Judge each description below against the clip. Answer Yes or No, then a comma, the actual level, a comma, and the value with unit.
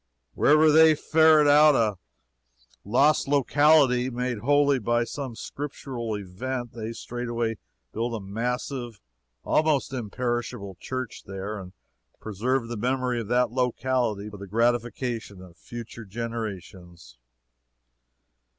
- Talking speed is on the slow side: Yes, slow, 115 wpm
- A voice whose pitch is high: No, low, 120 Hz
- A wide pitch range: No, average, 3.5 semitones